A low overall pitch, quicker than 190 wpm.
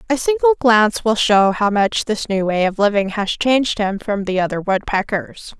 No: high, 215 Hz; fast, 205 wpm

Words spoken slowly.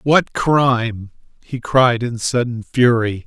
Yes: slow, 130 wpm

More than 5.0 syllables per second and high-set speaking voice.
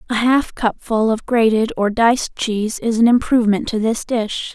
No: 4.9 syllables/s; high, 225 Hz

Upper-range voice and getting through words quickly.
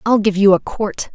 Yes: high, 200 Hz; fast, 260 wpm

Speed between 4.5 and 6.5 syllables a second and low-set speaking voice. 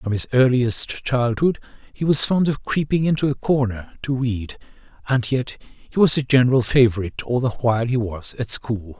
Yes: 5.0 syllables/s; low, 125 Hz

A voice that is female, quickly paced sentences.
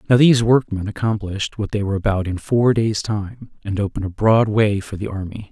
No: male; fast, 220 wpm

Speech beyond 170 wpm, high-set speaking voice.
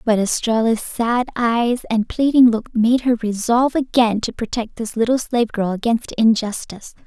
No: average, 160 wpm; high, 230 Hz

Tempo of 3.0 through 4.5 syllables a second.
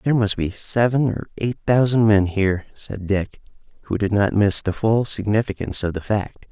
No: 5.0 syllables/s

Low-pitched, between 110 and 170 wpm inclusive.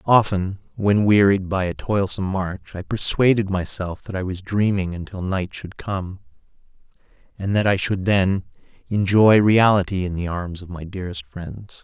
Yes: very low, 95 Hz; average, 160 wpm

